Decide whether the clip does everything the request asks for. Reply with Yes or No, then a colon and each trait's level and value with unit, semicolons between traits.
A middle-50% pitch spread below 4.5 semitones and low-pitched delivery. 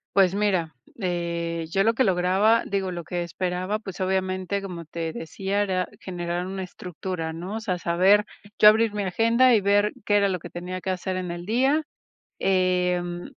No: narrow, 2.5 semitones; medium, 185 Hz